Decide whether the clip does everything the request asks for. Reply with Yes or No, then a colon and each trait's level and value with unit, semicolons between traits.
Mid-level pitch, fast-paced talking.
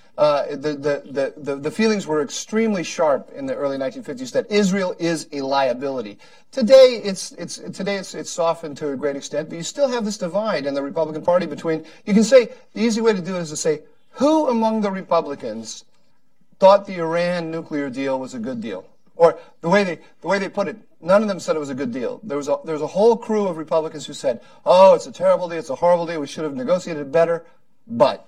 Yes: medium, 175 Hz; fast, 235 wpm